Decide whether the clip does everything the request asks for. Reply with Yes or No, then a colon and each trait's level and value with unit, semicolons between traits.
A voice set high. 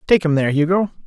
No: medium, 165 Hz